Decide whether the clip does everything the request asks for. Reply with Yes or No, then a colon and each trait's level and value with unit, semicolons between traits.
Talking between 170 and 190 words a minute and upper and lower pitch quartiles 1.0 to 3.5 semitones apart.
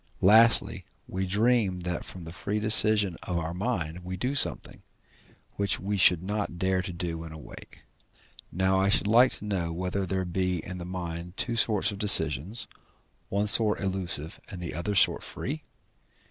Yes: average, 175 wpm; average, 2.9 semitones